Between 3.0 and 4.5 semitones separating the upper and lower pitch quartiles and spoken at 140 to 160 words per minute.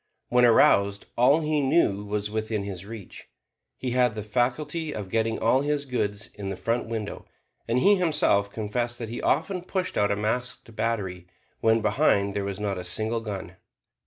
No: average, 3.6 semitones; average, 180 wpm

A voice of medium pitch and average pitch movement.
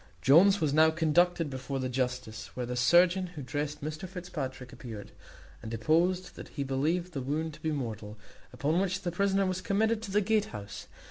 No: medium, 155 Hz; wide, 5.7 semitones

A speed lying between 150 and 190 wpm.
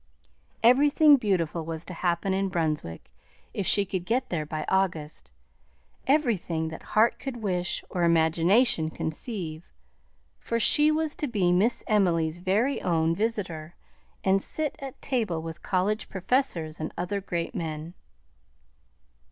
No: slow, 135 wpm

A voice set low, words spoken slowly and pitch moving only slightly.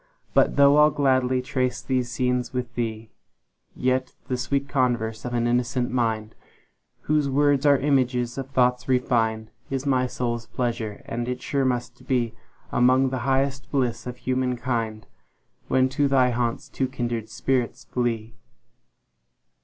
Yes: low, 125 Hz; slow, 130 wpm; narrow, 1.8 semitones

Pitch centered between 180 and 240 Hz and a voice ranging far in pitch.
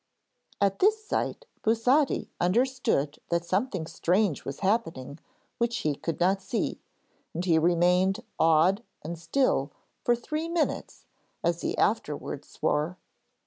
Yes: high, 190 Hz; wide, 6.3 semitones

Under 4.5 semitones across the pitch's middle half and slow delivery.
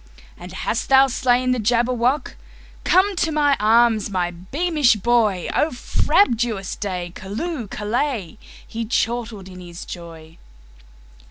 No: average, 5.2 semitones; slow, 105 wpm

